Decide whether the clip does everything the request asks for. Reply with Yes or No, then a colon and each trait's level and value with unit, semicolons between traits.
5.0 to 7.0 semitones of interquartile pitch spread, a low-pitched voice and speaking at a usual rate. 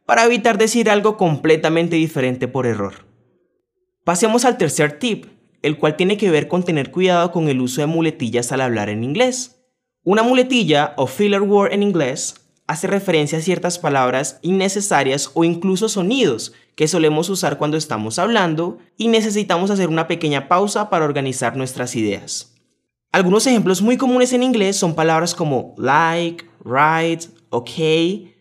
No: wide, 5.6 semitones; medium, 170 Hz; average, 155 wpm